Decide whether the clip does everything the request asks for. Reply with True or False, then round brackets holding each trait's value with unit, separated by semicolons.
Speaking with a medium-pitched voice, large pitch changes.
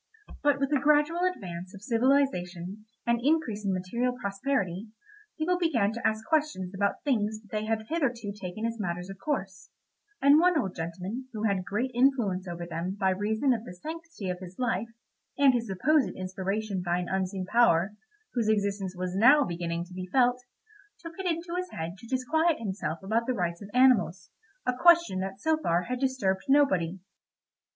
False (215 Hz; 6.4 semitones)